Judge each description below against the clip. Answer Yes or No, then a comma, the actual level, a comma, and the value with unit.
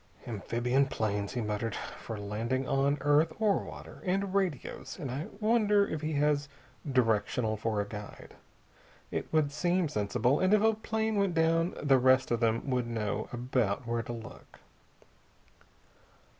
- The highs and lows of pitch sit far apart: Yes, wide, 6.5 semitones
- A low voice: Yes, low, 130 Hz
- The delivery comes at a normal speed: Yes, average, 150 wpm